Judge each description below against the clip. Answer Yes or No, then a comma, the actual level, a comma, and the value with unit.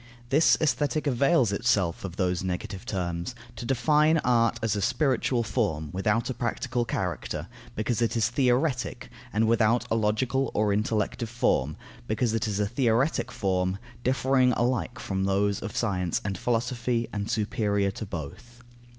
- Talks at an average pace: Yes, average, 155 wpm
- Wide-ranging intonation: No, average, 3.9 semitones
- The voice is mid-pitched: No, low, 115 Hz